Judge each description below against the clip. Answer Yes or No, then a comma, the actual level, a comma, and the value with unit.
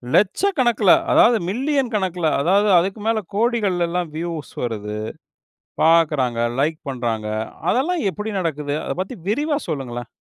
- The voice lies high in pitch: No, medium, 180 Hz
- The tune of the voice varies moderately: No, wide, 7.7 semitones